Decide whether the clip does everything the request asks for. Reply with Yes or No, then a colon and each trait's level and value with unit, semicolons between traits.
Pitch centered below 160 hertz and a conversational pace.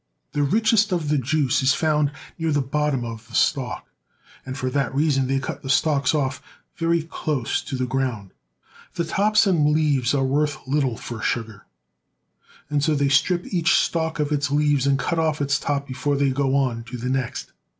Yes: medium, 140 Hz; average, 190 wpm